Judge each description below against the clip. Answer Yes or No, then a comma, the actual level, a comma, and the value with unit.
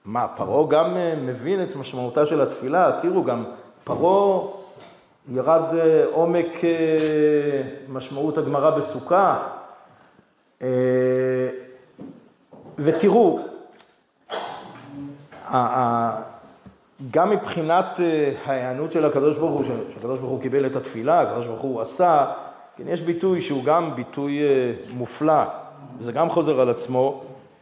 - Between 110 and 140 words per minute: No, slow, 100 wpm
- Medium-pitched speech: Yes, medium, 145 Hz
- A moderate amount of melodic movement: Yes, average, 4.1 semitones